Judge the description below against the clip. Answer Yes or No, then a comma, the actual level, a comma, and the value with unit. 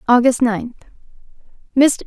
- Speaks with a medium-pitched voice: No, high, 245 Hz